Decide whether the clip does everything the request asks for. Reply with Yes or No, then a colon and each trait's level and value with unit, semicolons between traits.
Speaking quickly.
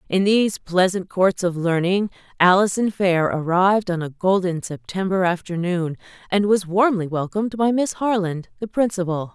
No: average, 150 wpm